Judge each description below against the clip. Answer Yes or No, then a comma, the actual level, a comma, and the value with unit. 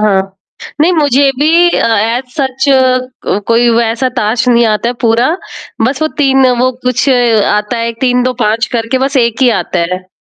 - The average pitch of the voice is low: No, high, 245 Hz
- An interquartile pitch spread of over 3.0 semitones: No, average, 2.7 semitones